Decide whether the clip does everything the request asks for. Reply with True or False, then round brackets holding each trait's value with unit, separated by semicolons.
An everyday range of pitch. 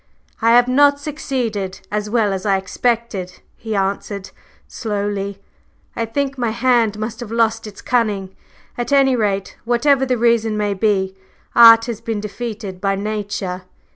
True (3.1 semitones)